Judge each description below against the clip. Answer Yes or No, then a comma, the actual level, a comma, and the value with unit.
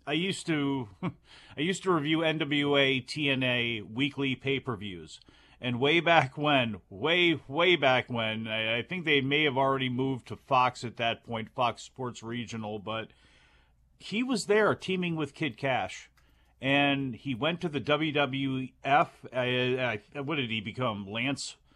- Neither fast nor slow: Yes, average, 160 wpm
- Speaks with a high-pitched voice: No, low, 135 Hz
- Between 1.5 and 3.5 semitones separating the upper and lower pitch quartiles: No, average, 4.2 semitones